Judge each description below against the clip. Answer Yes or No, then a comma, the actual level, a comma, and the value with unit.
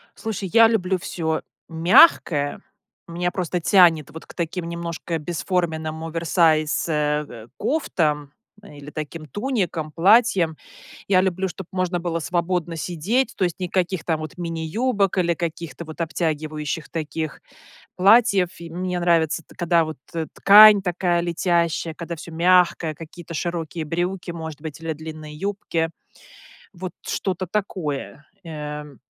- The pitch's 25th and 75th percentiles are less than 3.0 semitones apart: Yes, narrow, 2.6 semitones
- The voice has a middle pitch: Yes, medium, 170 Hz